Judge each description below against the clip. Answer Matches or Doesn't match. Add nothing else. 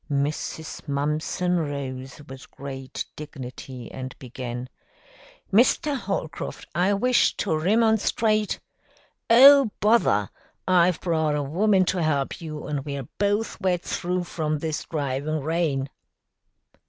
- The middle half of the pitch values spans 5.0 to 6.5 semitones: Matches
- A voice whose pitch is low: Doesn't match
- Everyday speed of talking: Doesn't match